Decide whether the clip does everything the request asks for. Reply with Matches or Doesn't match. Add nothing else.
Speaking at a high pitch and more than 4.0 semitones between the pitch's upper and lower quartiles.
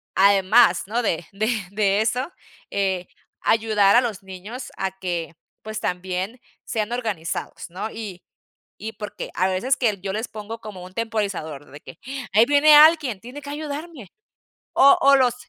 Matches